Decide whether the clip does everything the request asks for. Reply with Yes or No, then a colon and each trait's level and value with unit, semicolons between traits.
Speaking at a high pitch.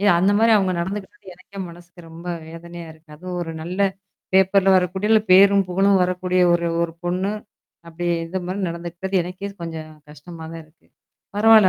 No: medium, 180 Hz